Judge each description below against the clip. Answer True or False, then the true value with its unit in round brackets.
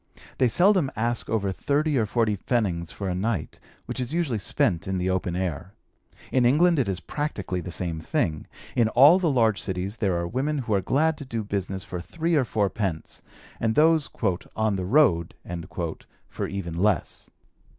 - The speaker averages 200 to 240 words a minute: False (180 wpm)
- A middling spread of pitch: False (6.6 semitones)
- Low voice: True (110 Hz)